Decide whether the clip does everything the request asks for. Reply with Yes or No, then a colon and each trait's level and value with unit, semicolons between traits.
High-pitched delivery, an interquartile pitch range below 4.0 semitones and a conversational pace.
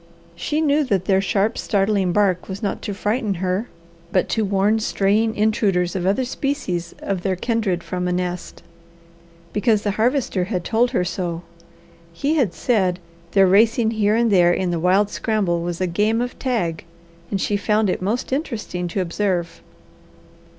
Yes: high, 200 Hz; average, 3.6 semitones; average, 165 wpm